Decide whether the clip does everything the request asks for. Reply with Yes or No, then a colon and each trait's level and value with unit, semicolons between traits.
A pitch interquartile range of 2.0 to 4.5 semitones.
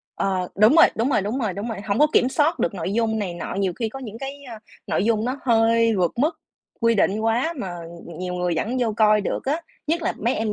Yes: average, 4.0 semitones